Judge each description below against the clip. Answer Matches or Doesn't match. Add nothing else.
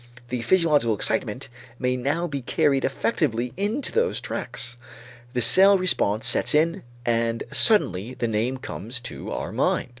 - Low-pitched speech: Matches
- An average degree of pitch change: Doesn't match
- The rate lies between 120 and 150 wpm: Matches